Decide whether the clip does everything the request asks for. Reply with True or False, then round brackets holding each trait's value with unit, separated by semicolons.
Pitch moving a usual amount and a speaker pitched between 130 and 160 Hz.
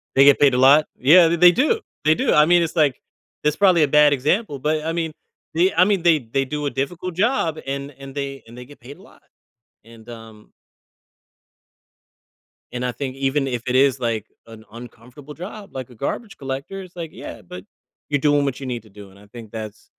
True (4.8 semitones; 140 Hz)